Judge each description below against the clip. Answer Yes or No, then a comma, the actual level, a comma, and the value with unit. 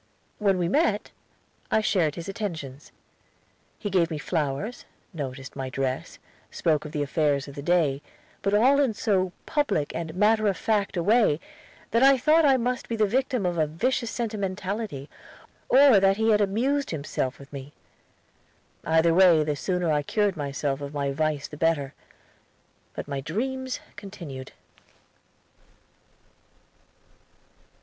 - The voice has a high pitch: No, medium, 180 Hz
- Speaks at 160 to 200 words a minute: No, average, 145 wpm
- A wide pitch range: Yes, wide, 6.8 semitones